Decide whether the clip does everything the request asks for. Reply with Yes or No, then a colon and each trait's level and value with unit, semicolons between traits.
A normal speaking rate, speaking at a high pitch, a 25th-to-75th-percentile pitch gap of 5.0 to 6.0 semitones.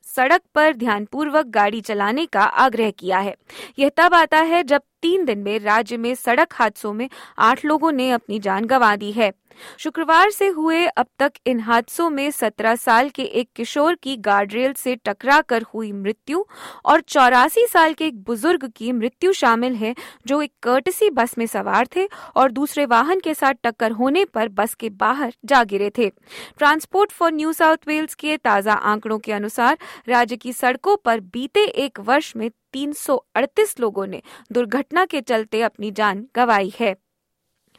Yes: average, 175 wpm; very high, 250 Hz; wide, 5.5 semitones